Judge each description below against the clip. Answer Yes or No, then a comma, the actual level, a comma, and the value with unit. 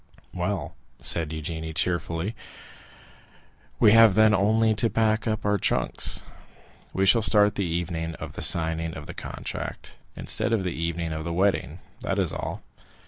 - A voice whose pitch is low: Yes, very low, 90 Hz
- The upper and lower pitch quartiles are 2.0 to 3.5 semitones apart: No, average, 4.5 semitones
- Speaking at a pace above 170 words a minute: No, average, 160 wpm